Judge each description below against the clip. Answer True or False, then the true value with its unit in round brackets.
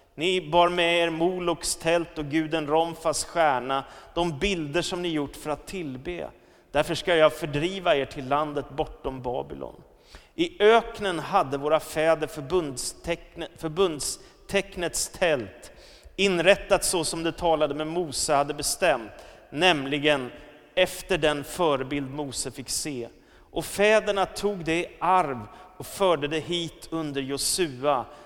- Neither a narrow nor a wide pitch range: True (3.0 semitones)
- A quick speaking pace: False (135 wpm)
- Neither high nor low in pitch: True (160 Hz)